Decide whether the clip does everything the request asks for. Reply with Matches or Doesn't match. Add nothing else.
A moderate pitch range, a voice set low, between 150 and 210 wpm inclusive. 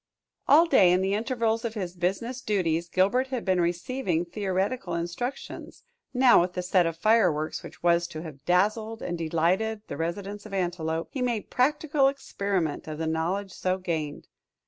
Doesn't match